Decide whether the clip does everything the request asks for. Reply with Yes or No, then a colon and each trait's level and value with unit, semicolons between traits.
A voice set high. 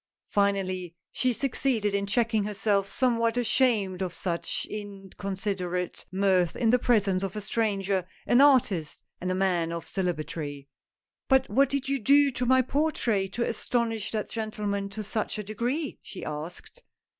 Yes: high, 205 Hz